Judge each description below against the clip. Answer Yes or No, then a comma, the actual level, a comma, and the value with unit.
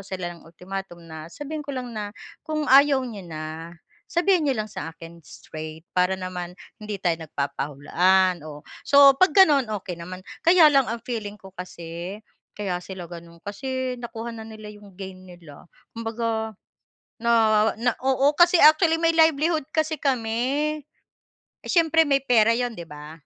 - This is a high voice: Yes, high, 215 Hz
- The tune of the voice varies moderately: No, wide, 7.5 semitones